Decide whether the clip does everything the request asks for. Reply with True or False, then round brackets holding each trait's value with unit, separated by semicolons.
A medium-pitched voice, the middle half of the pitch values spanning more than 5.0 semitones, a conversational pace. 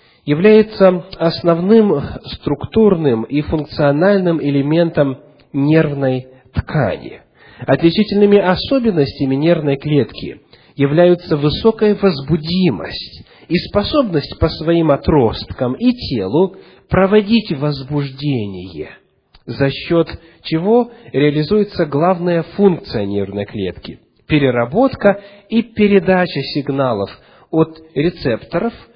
False (160 Hz; 5.6 semitones; 80 wpm)